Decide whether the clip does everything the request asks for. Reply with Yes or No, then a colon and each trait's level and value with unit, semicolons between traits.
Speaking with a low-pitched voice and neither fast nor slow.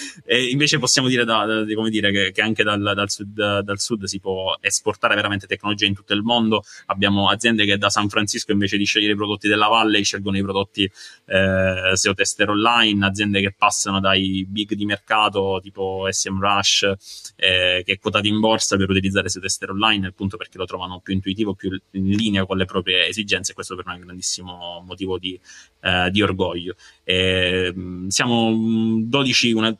No: low, 100 Hz; fast, 190 wpm